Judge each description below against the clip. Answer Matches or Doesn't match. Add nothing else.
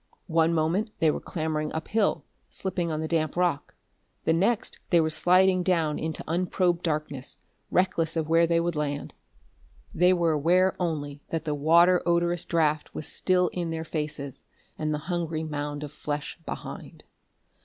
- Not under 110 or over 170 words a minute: Matches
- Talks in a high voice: Doesn't match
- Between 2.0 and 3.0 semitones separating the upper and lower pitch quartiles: Matches